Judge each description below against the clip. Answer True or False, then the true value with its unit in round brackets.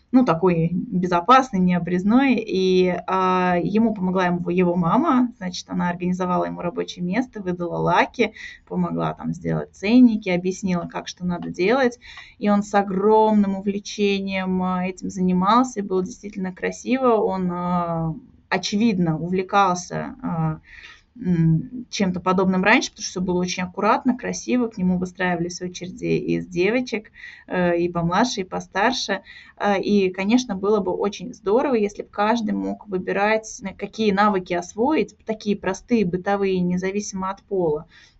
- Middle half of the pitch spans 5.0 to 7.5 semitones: False (3.2 semitones)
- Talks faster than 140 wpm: False (125 wpm)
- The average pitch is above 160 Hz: True (190 Hz)